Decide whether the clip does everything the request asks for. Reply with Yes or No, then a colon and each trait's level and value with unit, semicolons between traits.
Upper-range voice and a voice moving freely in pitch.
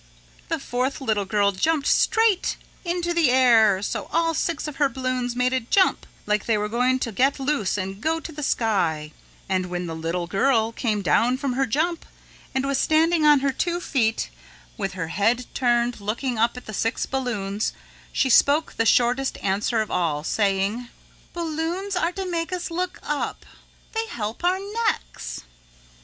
Yes: very high, 250 Hz; wide, 7.0 semitones